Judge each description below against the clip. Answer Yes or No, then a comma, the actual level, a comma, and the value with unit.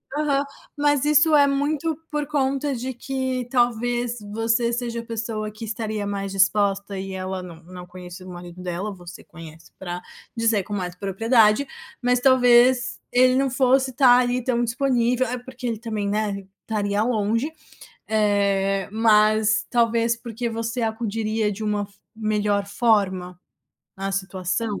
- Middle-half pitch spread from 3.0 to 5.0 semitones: Yes, average, 3.7 semitones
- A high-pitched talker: Yes, high, 225 Hz